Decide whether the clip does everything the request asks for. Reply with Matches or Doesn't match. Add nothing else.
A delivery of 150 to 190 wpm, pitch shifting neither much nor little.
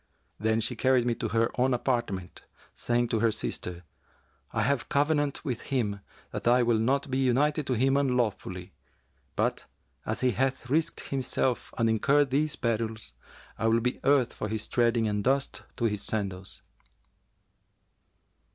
Matches